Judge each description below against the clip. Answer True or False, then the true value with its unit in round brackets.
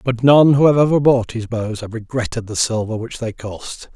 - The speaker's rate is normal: False (230 wpm)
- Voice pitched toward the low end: True (120 Hz)